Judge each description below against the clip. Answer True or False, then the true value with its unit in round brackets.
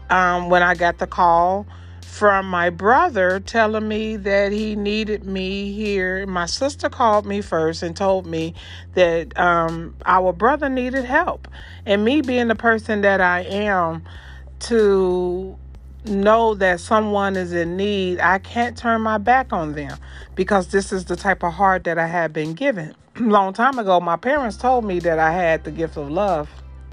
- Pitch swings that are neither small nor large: True (4.2 semitones)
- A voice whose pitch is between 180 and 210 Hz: True (185 Hz)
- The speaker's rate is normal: True (175 wpm)